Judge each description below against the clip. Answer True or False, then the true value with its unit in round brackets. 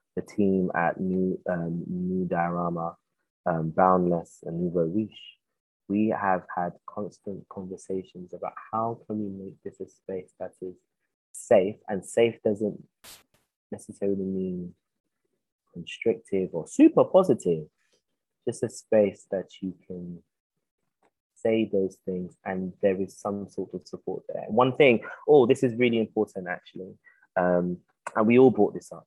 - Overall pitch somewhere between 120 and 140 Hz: False (95 Hz)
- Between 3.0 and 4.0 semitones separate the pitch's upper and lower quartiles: True (3.4 semitones)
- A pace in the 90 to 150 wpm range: True (140 wpm)